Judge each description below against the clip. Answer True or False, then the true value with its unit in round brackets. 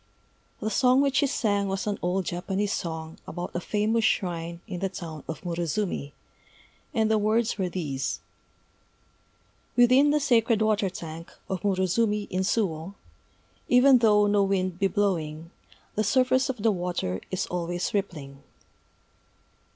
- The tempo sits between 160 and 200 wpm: False (145 wpm)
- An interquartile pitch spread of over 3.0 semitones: True (4.0 semitones)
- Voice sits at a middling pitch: False (195 Hz)